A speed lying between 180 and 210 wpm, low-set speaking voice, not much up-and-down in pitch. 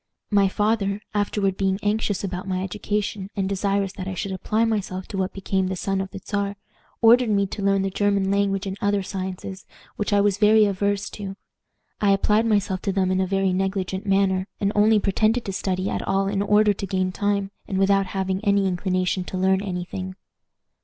No: average, 200 wpm; high, 195 Hz; narrow, 1.3 semitones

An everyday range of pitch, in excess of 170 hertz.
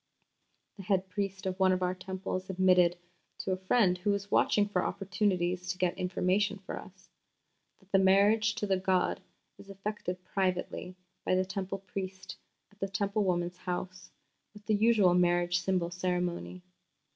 No: narrow, 1.5 semitones; medium, 185 Hz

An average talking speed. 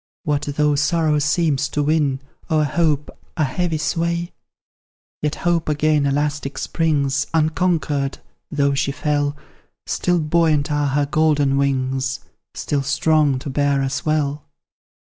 No: slow, 125 wpm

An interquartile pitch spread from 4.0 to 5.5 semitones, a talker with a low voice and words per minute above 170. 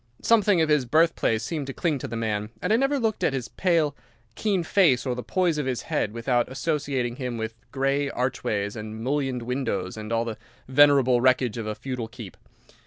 Yes: average, 4.5 semitones; low, 130 Hz; average, 200 wpm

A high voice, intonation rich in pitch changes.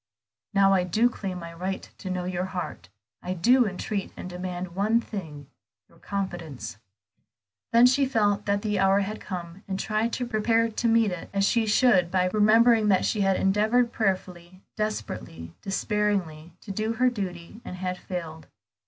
No: high, 195 Hz; average, 3.2 semitones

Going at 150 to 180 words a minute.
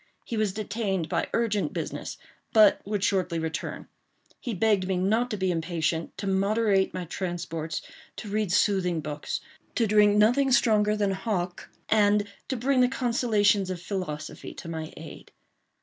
No: slow, 135 wpm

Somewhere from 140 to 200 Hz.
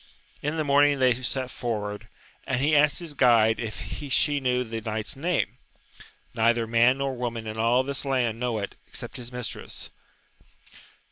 No: low, 125 Hz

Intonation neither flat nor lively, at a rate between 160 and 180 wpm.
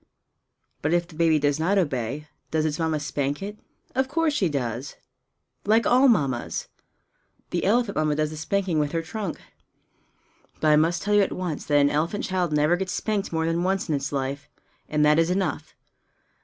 No: average, 4.5 semitones; average, 190 wpm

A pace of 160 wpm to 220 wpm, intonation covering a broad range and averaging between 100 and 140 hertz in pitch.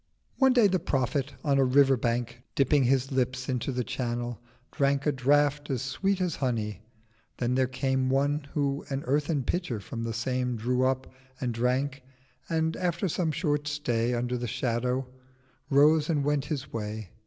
No: average, 170 wpm; average, 2.9 semitones; low, 135 Hz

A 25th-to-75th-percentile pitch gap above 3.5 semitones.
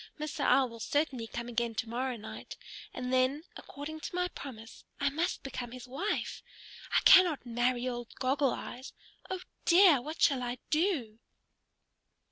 Yes: average, 4.0 semitones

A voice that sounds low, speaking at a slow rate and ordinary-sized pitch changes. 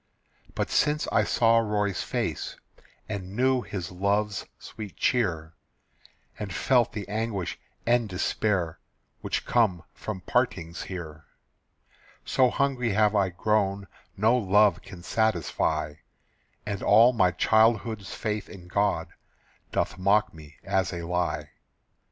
Yes: low, 105 Hz; slow, 120 wpm; average, 3.5 semitones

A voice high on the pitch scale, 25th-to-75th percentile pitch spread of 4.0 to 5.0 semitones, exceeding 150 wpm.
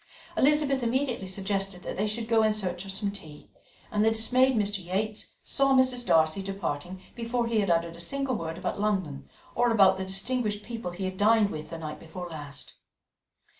Yes: high, 200 Hz; average, 4.5 semitones; average, 190 wpm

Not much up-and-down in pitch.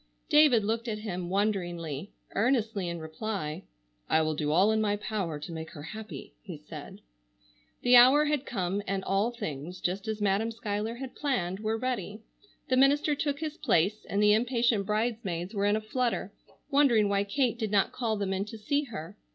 No: average, 4.1 semitones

